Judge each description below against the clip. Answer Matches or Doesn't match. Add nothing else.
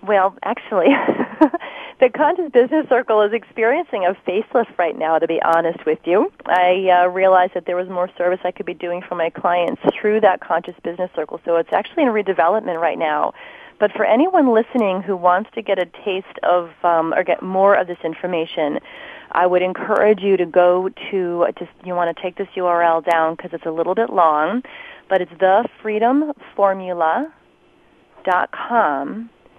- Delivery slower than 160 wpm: Doesn't match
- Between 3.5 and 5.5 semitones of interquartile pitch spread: Matches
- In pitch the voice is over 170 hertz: Matches